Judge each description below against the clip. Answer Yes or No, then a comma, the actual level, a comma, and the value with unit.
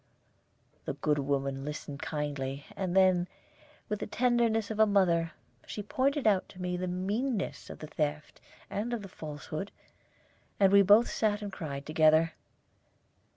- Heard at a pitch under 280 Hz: Yes, medium, 185 Hz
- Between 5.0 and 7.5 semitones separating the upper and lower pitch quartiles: Yes, wide, 5.5 semitones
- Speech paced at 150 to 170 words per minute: Yes, average, 155 wpm